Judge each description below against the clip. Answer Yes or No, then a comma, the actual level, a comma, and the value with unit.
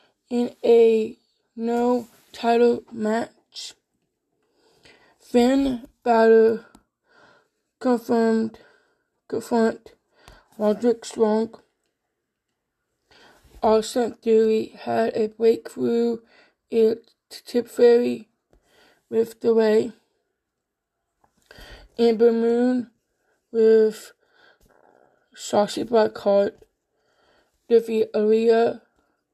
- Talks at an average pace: No, slow, 60 wpm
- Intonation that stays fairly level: Yes, narrow, 1.7 semitones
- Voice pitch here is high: Yes, high, 230 Hz